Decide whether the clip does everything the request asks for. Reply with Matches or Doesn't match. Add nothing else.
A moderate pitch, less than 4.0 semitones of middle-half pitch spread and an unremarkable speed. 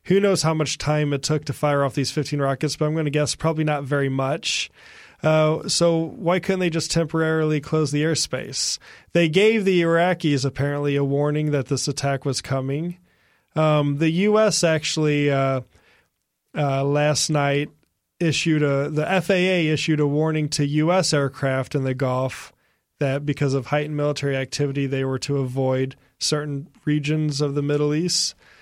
Matches